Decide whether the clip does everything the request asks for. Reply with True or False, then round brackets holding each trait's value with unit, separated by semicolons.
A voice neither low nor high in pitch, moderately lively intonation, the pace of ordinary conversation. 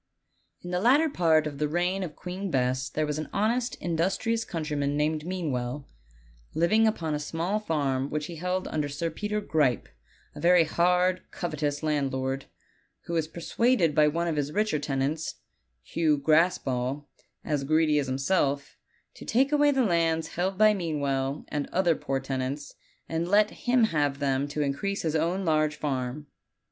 True (155 Hz; 4.0 semitones; 170 wpm)